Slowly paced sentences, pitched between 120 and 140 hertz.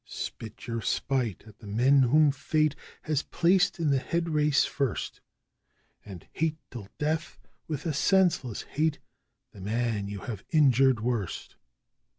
No: average, 145 wpm; low, 135 Hz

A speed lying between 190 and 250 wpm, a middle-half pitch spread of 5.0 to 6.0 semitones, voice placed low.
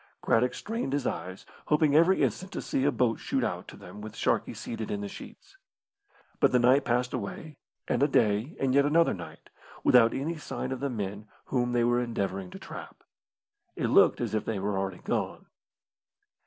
Yes: average, 195 wpm; average, 5.3 semitones; low, 125 Hz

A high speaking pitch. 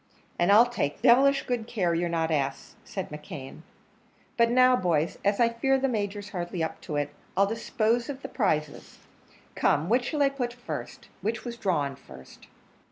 Yes: high, 205 Hz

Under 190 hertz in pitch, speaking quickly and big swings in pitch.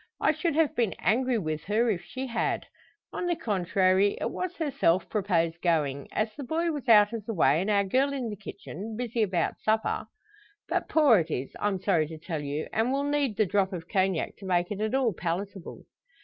No: high, 205 Hz; fast, 210 wpm; wide, 5.9 semitones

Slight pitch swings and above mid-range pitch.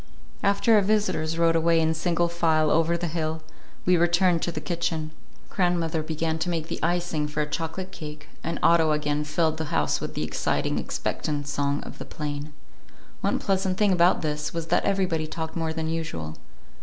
No: narrow, 1.9 semitones; medium, 165 Hz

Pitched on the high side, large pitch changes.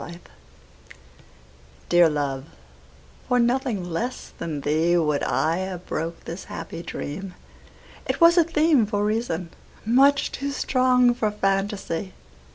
Yes: high, 195 Hz; wide, 6.8 semitones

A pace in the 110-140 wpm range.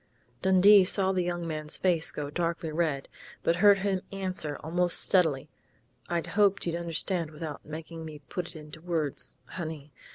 No: average, 160 wpm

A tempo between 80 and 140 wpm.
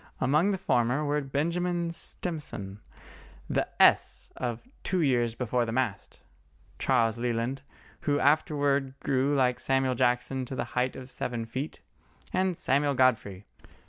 Yes: slow, 135 wpm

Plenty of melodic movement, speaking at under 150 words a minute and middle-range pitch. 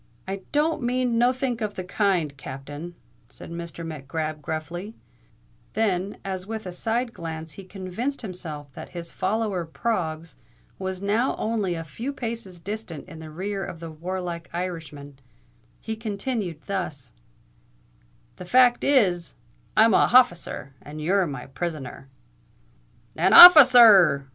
Yes: wide, 5.7 semitones; slow, 135 wpm; medium, 180 Hz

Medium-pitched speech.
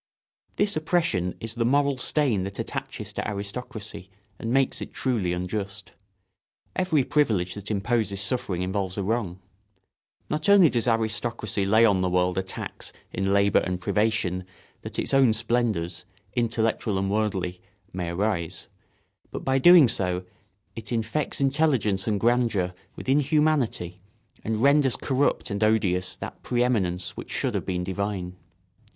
No: low, 110 Hz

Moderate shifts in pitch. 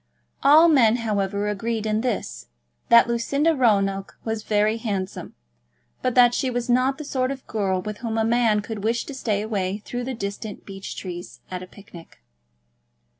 Yes: average, 3.4 semitones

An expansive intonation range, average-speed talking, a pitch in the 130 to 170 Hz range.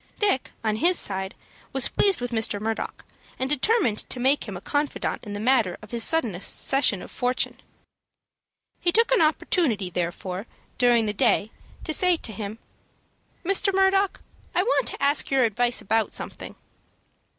No: wide, 7.3 semitones; average, 160 wpm; high, 245 Hz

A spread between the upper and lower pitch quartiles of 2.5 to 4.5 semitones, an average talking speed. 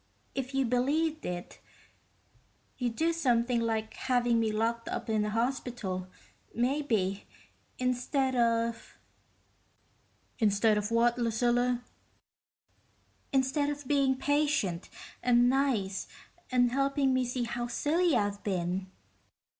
No: average, 3.3 semitones; slow, 110 wpm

